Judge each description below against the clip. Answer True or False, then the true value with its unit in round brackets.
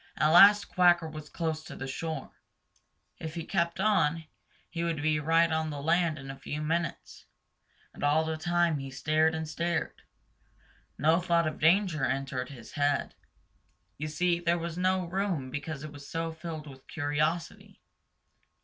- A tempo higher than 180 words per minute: False (165 wpm)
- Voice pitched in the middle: True (160 Hz)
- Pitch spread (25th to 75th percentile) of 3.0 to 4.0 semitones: False (2.4 semitones)